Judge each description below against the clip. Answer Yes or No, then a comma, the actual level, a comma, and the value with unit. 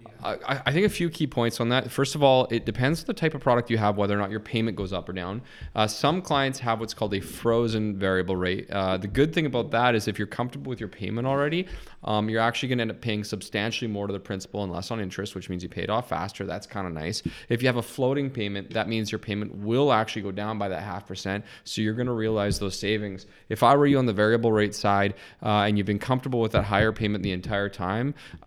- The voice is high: No, low, 110 Hz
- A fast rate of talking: Yes, fast, 270 wpm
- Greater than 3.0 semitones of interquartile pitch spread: Yes, average, 3.4 semitones